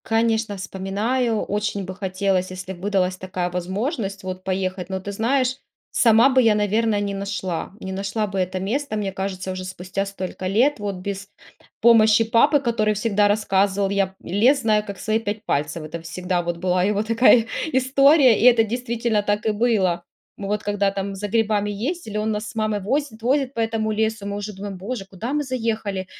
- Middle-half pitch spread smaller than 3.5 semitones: Yes, average, 3.0 semitones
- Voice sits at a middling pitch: No, high, 205 Hz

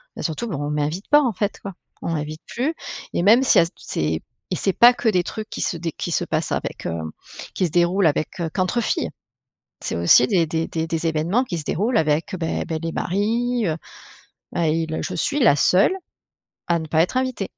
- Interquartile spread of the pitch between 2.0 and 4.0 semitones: No, average, 5.1 semitones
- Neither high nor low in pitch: Yes, medium, 170 Hz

